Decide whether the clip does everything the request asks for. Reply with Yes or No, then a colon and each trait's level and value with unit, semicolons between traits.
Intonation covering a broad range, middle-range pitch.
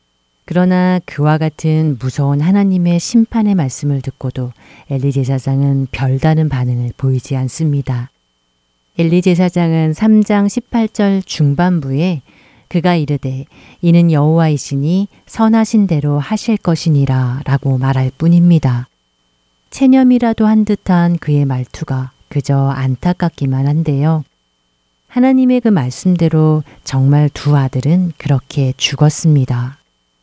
No: average, 5.0 semitones; medium, 145 Hz